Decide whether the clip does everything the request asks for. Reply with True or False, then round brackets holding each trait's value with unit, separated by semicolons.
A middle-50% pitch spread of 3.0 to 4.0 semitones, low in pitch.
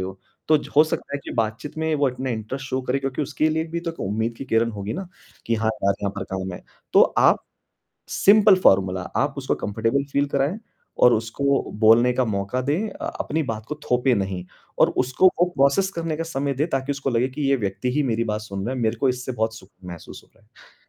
False (4.4 semitones; 125 Hz)